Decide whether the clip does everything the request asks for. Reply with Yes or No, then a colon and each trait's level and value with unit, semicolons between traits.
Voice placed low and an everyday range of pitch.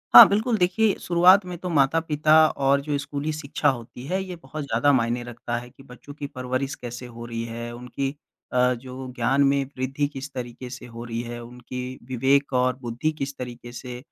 Yes: low, 130 Hz; average, 3.0 semitones